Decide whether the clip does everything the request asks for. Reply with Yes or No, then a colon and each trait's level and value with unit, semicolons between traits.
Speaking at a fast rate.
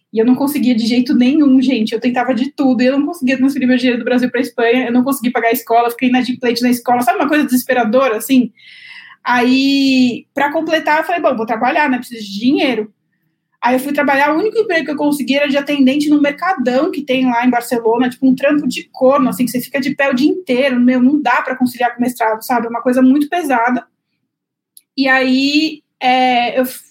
Yes: fast, 230 wpm